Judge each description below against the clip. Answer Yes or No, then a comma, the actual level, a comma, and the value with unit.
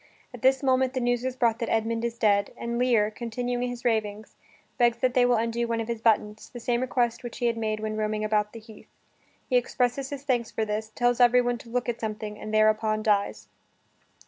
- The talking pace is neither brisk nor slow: No, fast, 220 wpm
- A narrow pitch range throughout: Yes, narrow, 2.2 semitones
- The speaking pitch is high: Yes, high, 235 Hz